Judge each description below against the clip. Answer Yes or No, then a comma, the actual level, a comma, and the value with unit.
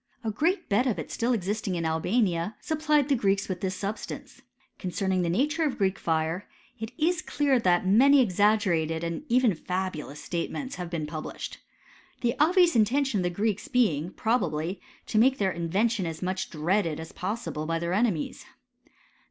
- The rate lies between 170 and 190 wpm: Yes, average, 180 wpm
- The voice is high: Yes, high, 195 Hz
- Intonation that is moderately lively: No, wide, 6.0 semitones